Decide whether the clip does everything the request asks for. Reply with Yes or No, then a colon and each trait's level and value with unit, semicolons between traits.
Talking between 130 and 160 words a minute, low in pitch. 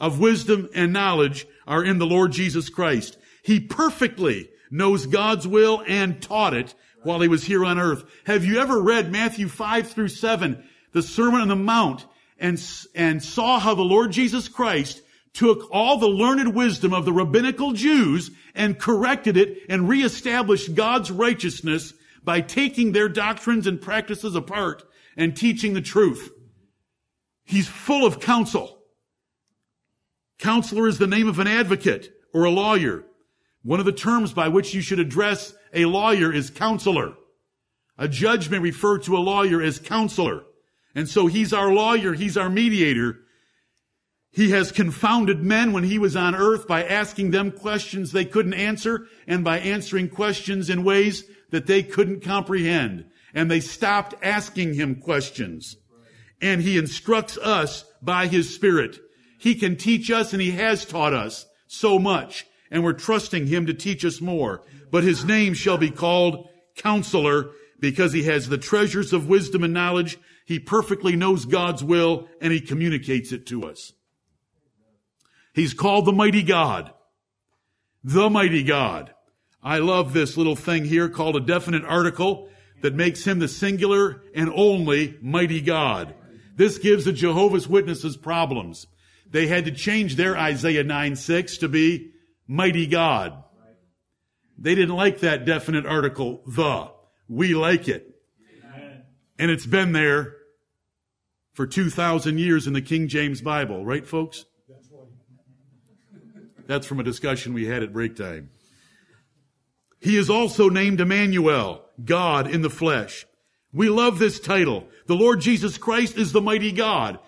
No: average, 155 wpm; medium, 180 Hz